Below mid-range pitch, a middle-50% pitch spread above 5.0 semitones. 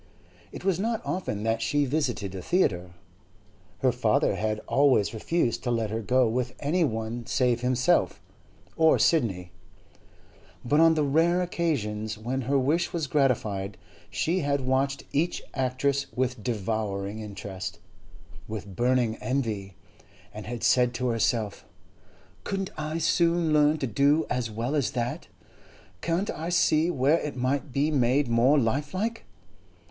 Yes: low, 130 Hz; wide, 5.5 semitones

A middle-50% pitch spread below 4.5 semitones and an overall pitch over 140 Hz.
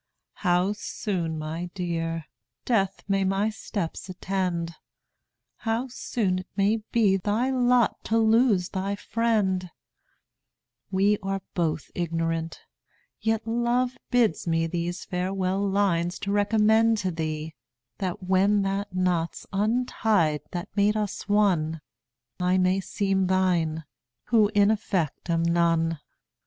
Yes: average, 3.5 semitones; high, 190 Hz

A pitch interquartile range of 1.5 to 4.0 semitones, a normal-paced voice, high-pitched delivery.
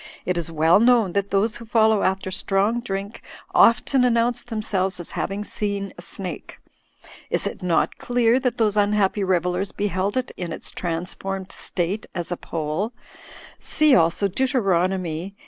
Yes: average, 3.7 semitones; average, 155 wpm; high, 195 Hz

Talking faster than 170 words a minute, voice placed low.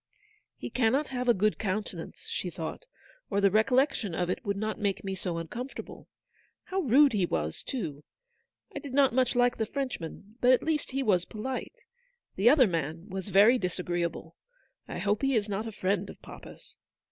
No: average, 190 wpm; high, 215 Hz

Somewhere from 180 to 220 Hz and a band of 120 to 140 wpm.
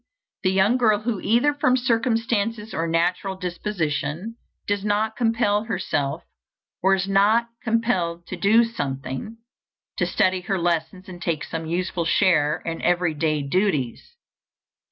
Yes: high, 190 Hz; slow, 135 wpm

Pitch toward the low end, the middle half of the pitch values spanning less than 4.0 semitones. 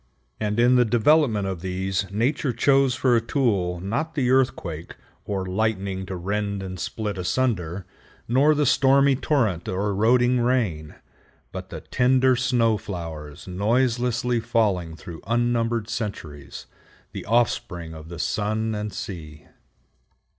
No: low, 110 Hz; average, 4.9 semitones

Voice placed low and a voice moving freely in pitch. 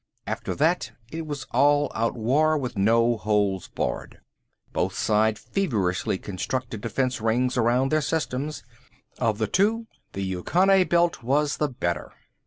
Yes: low, 125 Hz; wide, 5.7 semitones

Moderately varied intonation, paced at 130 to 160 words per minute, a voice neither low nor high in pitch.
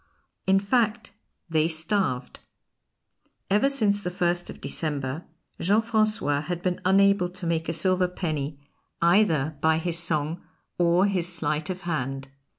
Yes: average, 3.7 semitones; average, 140 wpm; medium, 175 Hz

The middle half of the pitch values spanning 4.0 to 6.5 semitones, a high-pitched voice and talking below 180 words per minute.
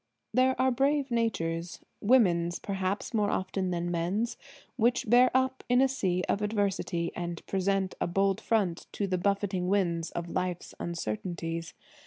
Yes: average, 5.1 semitones; high, 195 Hz; average, 140 wpm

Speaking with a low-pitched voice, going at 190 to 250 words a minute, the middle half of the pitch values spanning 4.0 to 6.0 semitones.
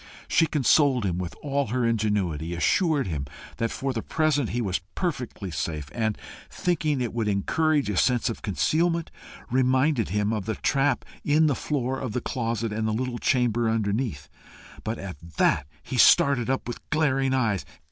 No: low, 120 Hz; average, 170 wpm; average, 4.9 semitones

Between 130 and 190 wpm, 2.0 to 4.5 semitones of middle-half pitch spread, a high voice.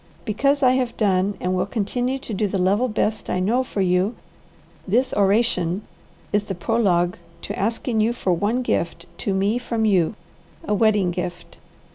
Yes: average, 170 wpm; average, 4.0 semitones; high, 205 Hz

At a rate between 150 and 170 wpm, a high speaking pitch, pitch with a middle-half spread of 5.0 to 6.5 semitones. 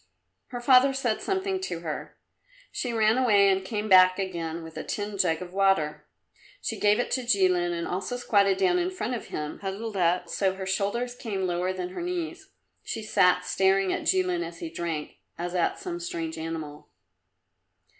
No: average, 185 wpm; high, 195 Hz; wide, 5.5 semitones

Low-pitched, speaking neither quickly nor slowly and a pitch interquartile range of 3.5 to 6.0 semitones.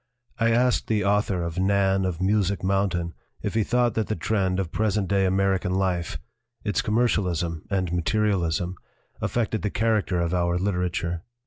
No: very low, 95 Hz; average, 160 wpm; average, 3.1 semitones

